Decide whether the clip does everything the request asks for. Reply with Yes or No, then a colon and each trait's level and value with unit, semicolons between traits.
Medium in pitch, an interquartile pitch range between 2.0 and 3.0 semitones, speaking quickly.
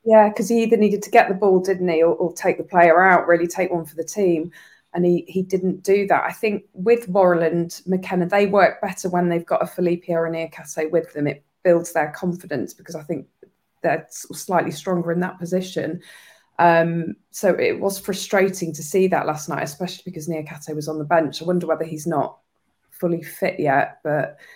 Yes: medium, 175 Hz; narrow, 2.6 semitones; fast, 210 wpm